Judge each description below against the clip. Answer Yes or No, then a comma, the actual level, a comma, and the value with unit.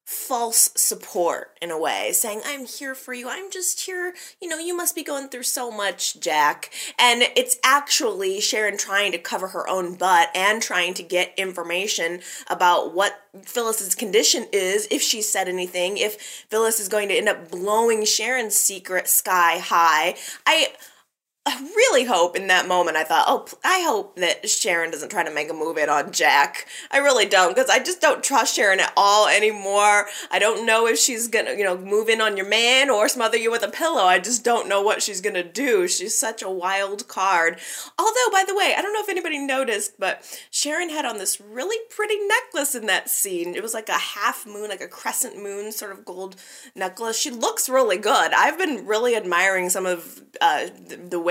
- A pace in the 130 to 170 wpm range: No, fast, 205 wpm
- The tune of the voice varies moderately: No, wide, 7.1 semitones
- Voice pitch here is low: No, high, 225 Hz